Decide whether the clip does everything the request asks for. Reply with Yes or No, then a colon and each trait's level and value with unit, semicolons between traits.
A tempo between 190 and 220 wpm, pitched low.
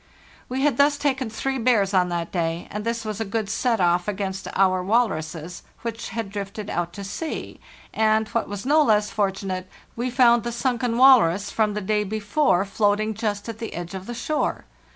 No: average, 195 wpm; high, 215 Hz